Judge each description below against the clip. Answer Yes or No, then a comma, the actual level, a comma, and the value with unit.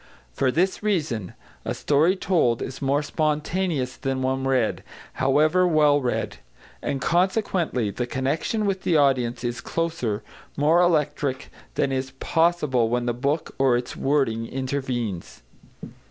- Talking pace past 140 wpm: No, slow, 135 wpm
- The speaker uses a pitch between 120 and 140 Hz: Yes, low, 135 Hz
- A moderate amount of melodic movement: Yes, average, 4.5 semitones